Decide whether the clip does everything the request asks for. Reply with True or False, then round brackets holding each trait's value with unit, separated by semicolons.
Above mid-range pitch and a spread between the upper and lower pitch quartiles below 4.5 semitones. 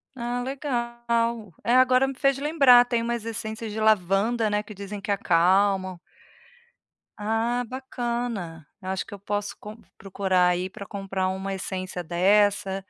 True (210 Hz; 3.7 semitones)